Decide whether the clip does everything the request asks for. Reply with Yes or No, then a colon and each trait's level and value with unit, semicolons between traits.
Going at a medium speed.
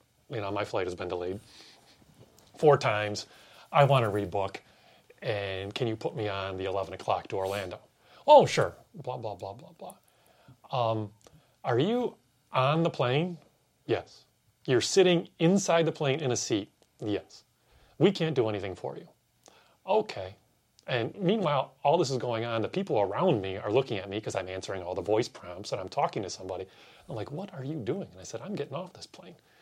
Yes: average, 190 wpm